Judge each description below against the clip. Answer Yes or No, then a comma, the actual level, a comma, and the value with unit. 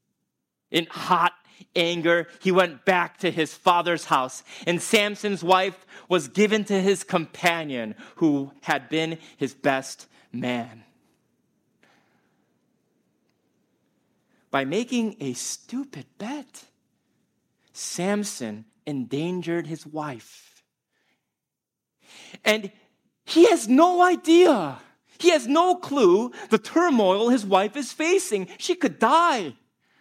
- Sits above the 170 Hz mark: Yes, medium, 185 Hz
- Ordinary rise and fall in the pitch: No, wide, 6.7 semitones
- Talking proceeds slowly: Yes, slow, 100 wpm